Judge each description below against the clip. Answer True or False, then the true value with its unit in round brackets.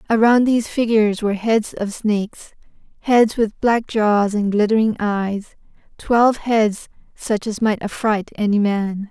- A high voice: True (215 Hz)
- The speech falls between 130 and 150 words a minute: True (145 wpm)